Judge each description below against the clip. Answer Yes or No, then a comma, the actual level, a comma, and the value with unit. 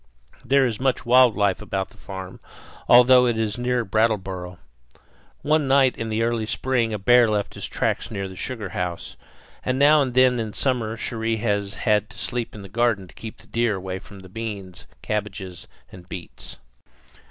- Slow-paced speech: No, average, 180 wpm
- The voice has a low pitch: Yes, low, 110 Hz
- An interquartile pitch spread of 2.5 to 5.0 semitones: Yes, average, 3.9 semitones